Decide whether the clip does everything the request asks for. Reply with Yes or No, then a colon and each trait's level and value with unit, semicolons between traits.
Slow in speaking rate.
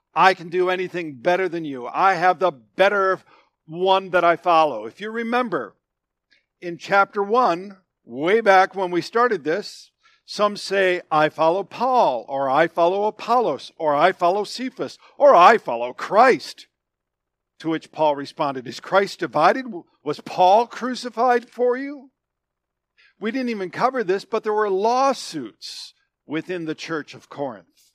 No: average, 150 wpm